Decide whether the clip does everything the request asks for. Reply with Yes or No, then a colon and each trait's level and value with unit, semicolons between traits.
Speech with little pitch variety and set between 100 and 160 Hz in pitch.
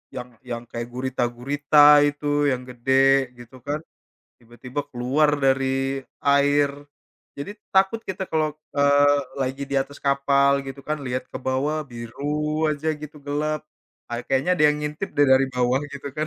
Yes: narrow, 2.2 semitones; medium, 140 Hz